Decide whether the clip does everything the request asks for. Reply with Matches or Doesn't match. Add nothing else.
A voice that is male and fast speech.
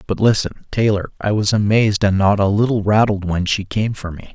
Matches